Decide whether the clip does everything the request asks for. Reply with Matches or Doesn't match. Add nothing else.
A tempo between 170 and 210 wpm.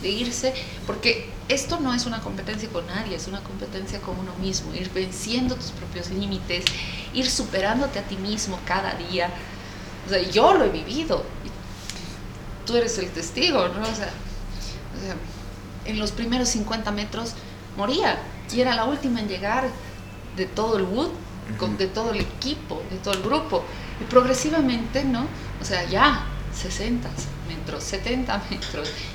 Doesn't match